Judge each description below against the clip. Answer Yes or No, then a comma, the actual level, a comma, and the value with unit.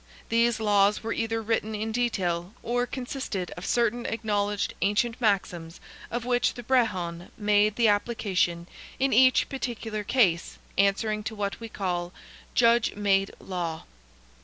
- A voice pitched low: No, high, 215 Hz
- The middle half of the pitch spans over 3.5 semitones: No, average, 3.2 semitones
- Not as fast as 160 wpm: Yes, slow, 135 wpm